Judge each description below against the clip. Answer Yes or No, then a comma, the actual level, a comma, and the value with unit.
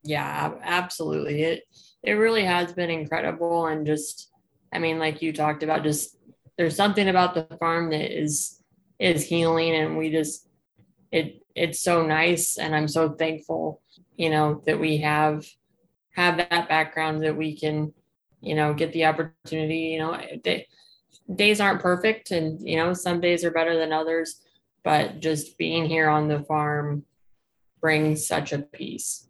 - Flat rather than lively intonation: Yes, narrow, 1.8 semitones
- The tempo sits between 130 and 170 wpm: Yes, average, 160 wpm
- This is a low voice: No, medium, 160 Hz